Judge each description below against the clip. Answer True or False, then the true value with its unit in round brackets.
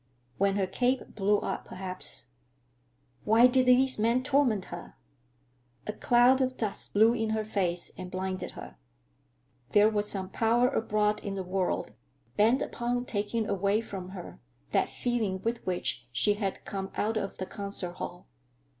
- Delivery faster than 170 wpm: False (155 wpm)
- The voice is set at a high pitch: True (205 Hz)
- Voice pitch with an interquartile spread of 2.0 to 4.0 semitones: True (3.6 semitones)